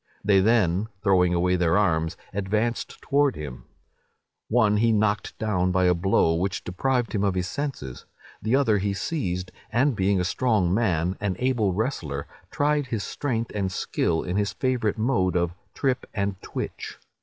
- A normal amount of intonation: Yes, average, 4.3 semitones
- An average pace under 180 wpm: Yes, average, 165 wpm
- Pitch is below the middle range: Yes, low, 100 Hz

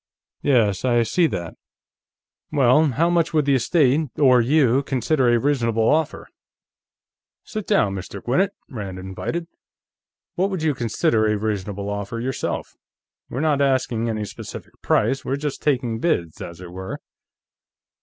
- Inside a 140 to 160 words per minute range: Yes, average, 145 wpm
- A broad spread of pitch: Yes, wide, 5.8 semitones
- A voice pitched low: Yes, low, 125 Hz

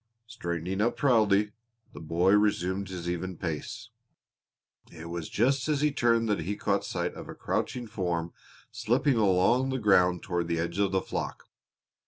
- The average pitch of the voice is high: No, low, 100 Hz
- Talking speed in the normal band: Yes, average, 165 wpm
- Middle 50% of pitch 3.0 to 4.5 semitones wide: No, average, 5.1 semitones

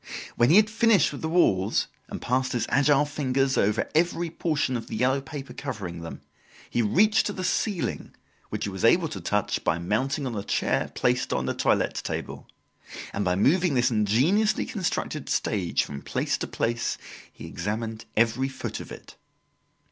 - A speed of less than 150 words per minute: No, average, 180 wpm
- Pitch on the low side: Yes, low, 130 Hz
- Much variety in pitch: Yes, wide, 6.9 semitones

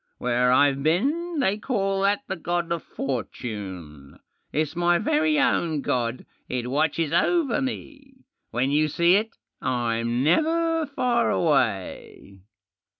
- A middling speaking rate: No, slow, 125 wpm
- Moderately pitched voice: Yes, medium, 165 Hz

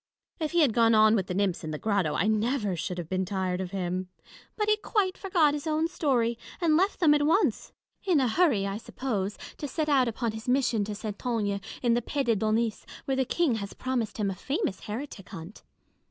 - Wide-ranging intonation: Yes, wide, 6.7 semitones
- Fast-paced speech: Yes, fast, 220 wpm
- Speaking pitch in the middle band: No, high, 230 Hz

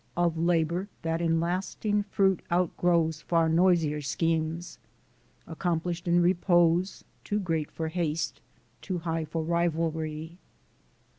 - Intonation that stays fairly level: Yes, narrow, 1.6 semitones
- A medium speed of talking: No, slow, 115 wpm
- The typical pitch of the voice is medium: Yes, medium, 170 Hz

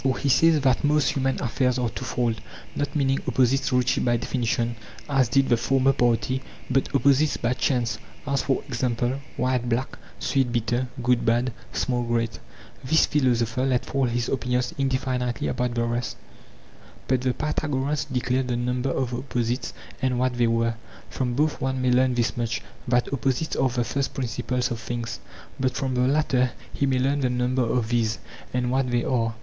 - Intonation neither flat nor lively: No, narrow, 1.7 semitones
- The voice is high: No, low, 125 Hz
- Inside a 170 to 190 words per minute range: Yes, average, 175 wpm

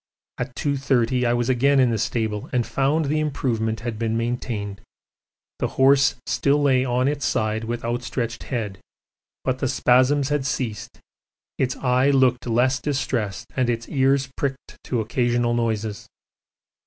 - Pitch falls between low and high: No, low, 125 Hz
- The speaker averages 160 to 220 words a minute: No, average, 150 wpm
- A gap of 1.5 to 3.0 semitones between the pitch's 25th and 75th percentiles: Yes, narrow, 2.5 semitones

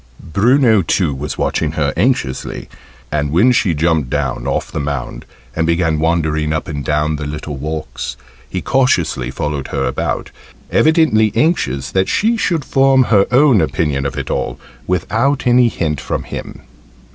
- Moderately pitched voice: No, very low, 80 Hz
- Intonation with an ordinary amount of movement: No, wide, 8.3 semitones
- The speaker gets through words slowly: No, average, 160 wpm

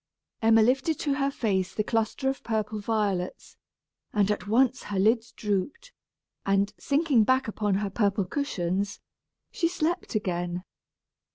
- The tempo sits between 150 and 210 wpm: No, slow, 135 wpm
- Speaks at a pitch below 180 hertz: No, high, 215 Hz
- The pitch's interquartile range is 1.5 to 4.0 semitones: No, average, 4.9 semitones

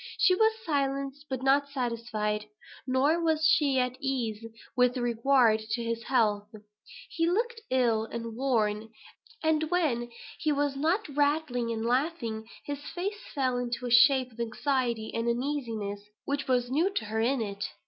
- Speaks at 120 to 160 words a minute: Yes, average, 155 wpm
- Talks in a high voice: Yes, very high, 255 Hz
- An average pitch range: Yes, average, 3.9 semitones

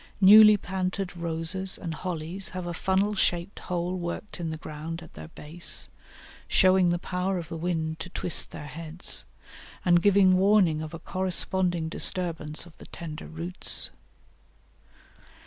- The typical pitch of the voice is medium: Yes, medium, 175 Hz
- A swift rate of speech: No, average, 145 wpm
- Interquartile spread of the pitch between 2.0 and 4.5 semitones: Yes, narrow, 2.4 semitones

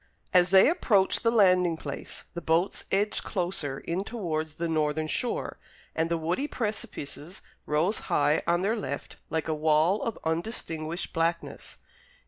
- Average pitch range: Yes, average, 3.9 semitones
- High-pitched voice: No, medium, 170 Hz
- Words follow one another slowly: No, average, 145 wpm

